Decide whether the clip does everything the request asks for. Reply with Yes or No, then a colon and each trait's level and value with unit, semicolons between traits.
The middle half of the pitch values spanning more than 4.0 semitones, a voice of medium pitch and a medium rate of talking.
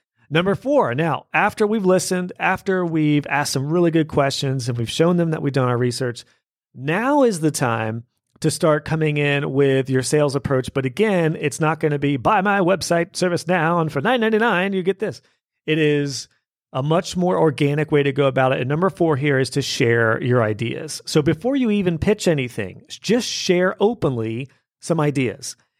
Yes: average, 5.1 semitones; medium, 155 Hz; average, 195 wpm